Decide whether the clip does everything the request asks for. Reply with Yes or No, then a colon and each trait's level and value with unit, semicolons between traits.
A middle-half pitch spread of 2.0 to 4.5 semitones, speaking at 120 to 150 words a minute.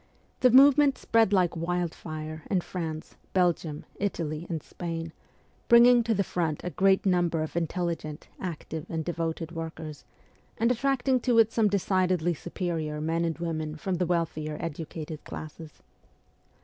Yes: average, 3.4 semitones; average, 145 wpm